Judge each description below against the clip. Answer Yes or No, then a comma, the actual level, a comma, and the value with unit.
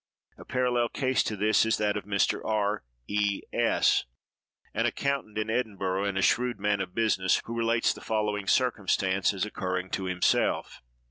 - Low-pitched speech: Yes, low, 105 Hz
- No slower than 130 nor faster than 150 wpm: No, average, 165 wpm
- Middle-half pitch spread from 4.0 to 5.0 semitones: No, average, 2.8 semitones